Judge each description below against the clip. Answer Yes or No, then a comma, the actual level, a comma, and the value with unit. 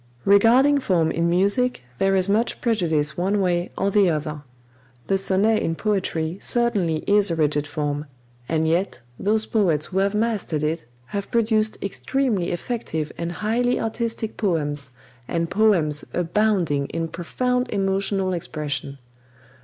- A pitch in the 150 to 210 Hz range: Yes, high, 190 Hz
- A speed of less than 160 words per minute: Yes, average, 140 wpm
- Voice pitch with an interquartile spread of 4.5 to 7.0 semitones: Yes, average, 5.0 semitones